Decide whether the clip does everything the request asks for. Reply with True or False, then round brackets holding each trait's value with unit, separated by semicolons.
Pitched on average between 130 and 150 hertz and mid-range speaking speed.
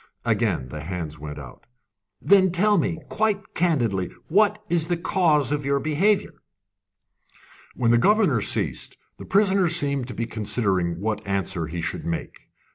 True (140 Hz; 150 wpm)